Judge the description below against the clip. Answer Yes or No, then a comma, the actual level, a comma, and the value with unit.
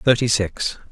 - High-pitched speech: No, low, 110 Hz